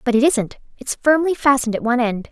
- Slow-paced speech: No, fast, 210 wpm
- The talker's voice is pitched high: Yes, very high, 255 Hz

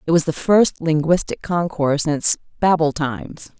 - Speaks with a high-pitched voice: No, medium, 160 Hz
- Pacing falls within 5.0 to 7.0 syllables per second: Yes, 5.1 syllables/s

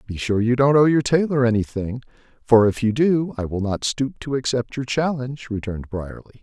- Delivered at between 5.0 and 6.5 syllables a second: Yes, 5.5 syllables/s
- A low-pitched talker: Yes, low, 120 Hz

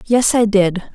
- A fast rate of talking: No, average, 190 wpm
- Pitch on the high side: Yes, high, 210 Hz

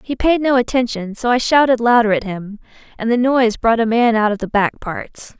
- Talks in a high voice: Yes, high, 230 Hz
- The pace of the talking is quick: Yes, fast, 235 wpm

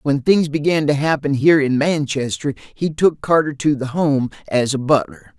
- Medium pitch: Yes, medium, 145 Hz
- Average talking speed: Yes, average, 190 wpm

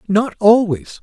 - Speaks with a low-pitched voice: No, high, 195 Hz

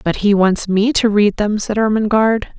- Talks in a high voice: Yes, high, 210 Hz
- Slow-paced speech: No, fast, 210 wpm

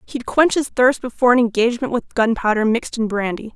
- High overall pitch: Yes, high, 235 Hz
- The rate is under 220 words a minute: Yes, average, 200 wpm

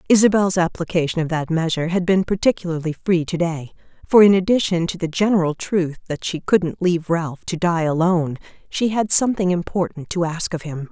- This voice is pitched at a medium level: Yes, medium, 175 Hz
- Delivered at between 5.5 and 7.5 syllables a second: Yes, 5.7 syllables/s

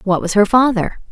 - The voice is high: Yes, high, 210 Hz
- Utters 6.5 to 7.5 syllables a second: No, 5.4 syllables/s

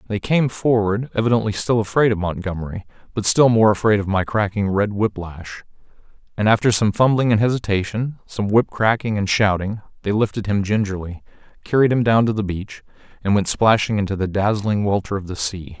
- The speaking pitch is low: Yes, low, 105 Hz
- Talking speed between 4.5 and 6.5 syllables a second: Yes, 5.5 syllables/s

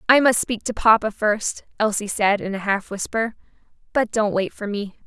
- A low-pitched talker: No, high, 210 Hz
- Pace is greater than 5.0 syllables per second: No, 4.9 syllables/s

